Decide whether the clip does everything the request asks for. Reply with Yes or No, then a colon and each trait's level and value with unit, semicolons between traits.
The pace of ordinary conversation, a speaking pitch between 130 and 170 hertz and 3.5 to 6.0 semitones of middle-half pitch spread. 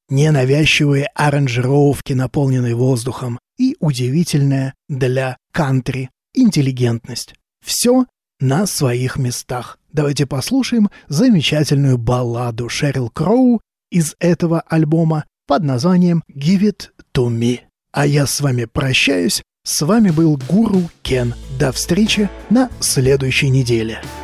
No: slow, 105 wpm; medium, 140 Hz; average, 4.8 semitones